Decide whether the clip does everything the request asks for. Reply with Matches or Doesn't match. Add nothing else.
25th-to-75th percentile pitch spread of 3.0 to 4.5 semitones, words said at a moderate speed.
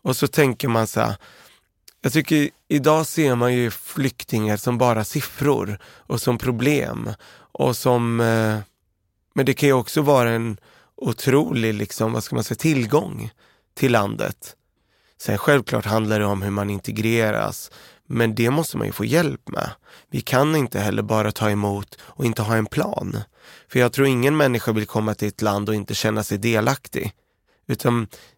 Matches